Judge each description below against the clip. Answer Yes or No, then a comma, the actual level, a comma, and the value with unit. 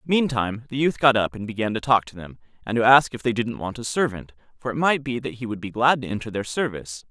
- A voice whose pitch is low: Yes, low, 120 Hz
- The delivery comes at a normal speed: No, fast, 280 wpm